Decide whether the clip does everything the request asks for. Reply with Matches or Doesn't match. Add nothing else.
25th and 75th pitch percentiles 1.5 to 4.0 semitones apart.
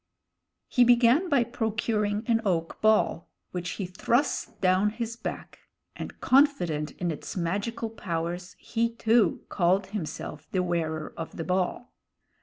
Doesn't match